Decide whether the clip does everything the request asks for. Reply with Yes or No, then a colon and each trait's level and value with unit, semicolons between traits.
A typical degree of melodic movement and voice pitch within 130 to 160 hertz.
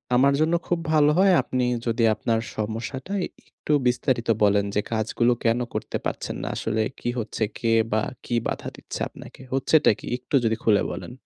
No: average, 3.6 semitones; low, 120 Hz